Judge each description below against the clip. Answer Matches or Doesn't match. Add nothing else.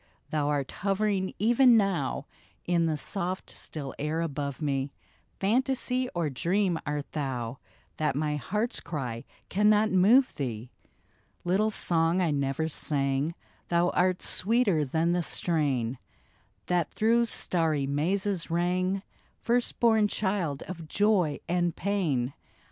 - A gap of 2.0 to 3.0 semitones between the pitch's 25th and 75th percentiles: Doesn't match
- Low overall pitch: Doesn't match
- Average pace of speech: Doesn't match